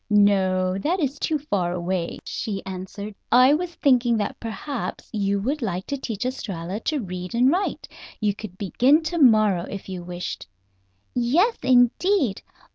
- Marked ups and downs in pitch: Yes, wide, 6.2 semitones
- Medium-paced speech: Yes, average, 155 wpm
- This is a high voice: Yes, high, 215 Hz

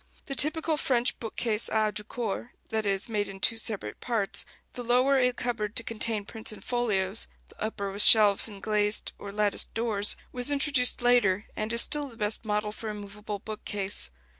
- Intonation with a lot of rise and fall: No, average, 2.7 semitones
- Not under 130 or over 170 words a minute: No, average, 190 wpm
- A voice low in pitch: No, high, 220 Hz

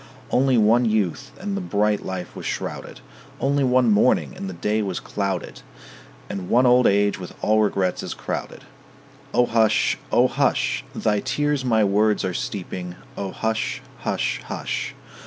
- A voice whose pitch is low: Yes, low, 105 Hz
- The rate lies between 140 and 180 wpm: Yes, average, 155 wpm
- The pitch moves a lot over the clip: No, average, 3.9 semitones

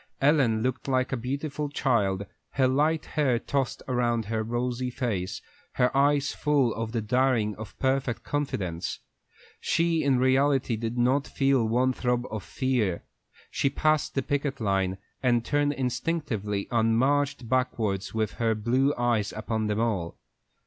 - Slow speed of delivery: No, average, 150 wpm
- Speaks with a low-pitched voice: Yes, low, 125 Hz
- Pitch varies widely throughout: No, average, 3.7 semitones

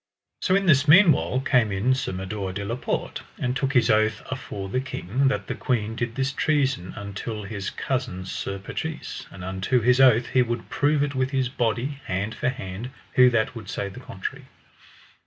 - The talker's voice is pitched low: Yes, low, 120 Hz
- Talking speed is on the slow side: No, average, 195 wpm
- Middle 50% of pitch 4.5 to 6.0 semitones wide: Yes, average, 4.8 semitones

